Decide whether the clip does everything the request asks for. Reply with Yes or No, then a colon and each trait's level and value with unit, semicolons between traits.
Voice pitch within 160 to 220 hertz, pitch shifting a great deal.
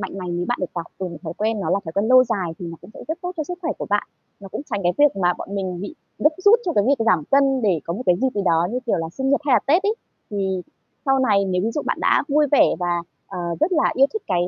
Yes: high, 205 Hz; wide, 7.4 semitones